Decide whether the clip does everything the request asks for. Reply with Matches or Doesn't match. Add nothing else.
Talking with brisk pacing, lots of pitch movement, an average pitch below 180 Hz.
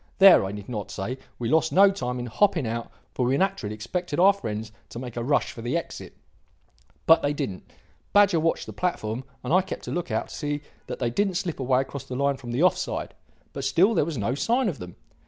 Matches